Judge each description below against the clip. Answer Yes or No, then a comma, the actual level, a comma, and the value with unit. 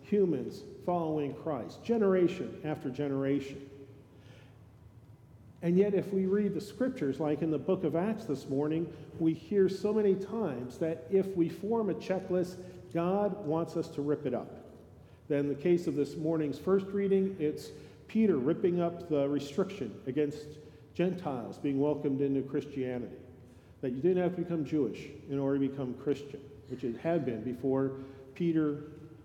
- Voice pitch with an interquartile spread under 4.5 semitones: No, average, 4.8 semitones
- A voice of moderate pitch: Yes, medium, 150 Hz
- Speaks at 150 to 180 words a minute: Yes, average, 160 wpm